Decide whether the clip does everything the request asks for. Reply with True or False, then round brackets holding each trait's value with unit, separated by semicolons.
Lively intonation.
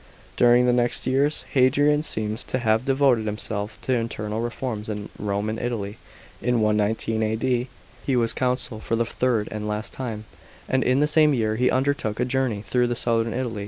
False (3.0 semitones)